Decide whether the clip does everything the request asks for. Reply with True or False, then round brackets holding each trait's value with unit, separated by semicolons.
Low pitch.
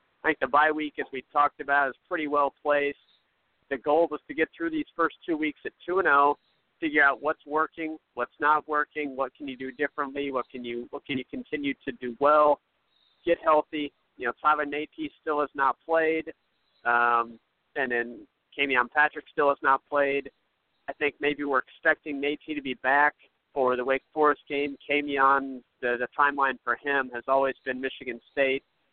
False (145 Hz)